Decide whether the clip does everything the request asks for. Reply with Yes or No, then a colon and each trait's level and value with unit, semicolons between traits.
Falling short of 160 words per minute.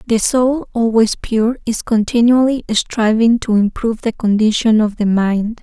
Yes: average, 150 wpm